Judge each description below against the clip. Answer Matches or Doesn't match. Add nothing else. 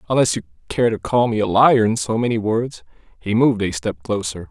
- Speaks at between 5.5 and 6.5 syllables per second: Matches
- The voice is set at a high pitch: Doesn't match